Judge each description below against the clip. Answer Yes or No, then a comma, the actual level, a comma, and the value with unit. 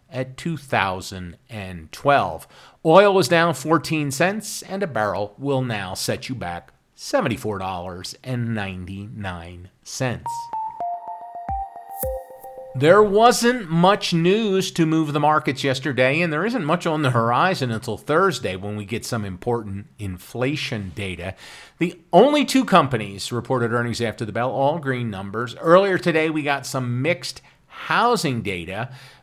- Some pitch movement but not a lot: No, wide, 8.5 semitones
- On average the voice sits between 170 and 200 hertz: No, low, 135 Hz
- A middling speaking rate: No, slow, 125 wpm